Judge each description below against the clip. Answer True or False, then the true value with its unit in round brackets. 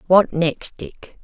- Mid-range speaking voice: True (160 Hz)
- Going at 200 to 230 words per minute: False (145 wpm)